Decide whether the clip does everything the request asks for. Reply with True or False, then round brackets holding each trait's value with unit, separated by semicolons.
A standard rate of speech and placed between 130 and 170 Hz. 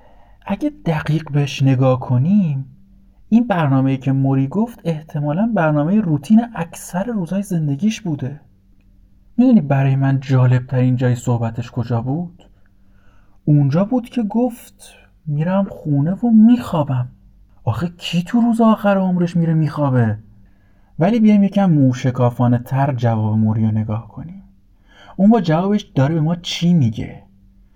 True (130 wpm; 140 Hz)